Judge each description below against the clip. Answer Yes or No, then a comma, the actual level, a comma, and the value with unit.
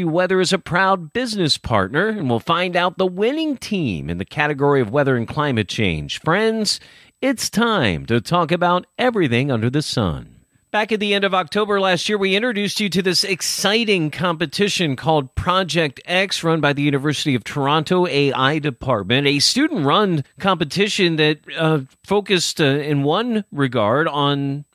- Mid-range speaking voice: Yes, medium, 165 Hz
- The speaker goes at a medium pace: Yes, average, 165 wpm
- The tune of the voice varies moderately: No, wide, 5.7 semitones